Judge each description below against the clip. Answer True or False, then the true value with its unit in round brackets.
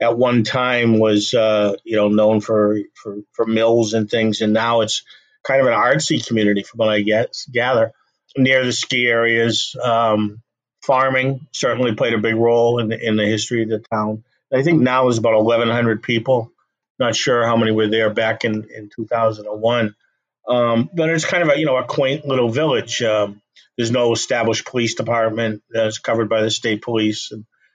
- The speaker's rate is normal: True (190 wpm)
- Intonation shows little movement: True (1.7 semitones)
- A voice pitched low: True (115 Hz)